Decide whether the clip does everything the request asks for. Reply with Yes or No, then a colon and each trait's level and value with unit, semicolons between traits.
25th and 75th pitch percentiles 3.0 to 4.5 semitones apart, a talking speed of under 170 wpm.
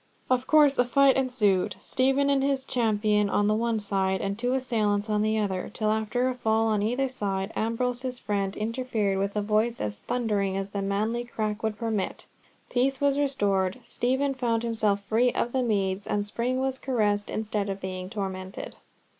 No: average, 3.7 semitones; average, 180 wpm